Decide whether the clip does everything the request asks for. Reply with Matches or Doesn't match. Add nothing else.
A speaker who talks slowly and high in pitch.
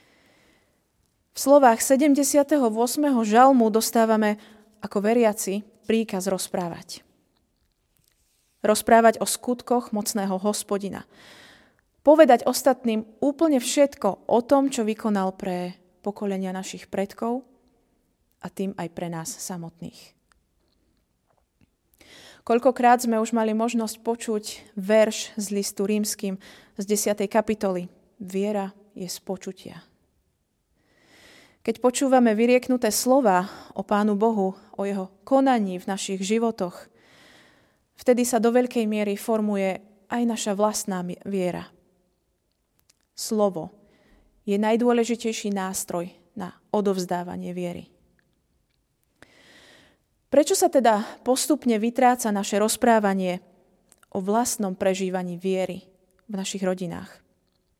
Matches